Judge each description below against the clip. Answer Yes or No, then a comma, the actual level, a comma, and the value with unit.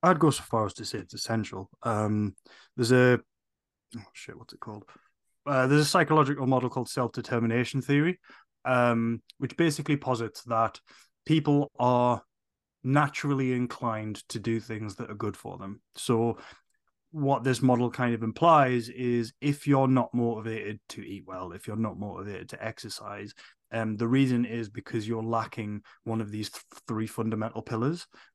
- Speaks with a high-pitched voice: No, low, 120 Hz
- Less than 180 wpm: Yes, average, 165 wpm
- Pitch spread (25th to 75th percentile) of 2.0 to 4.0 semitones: Yes, average, 2.9 semitones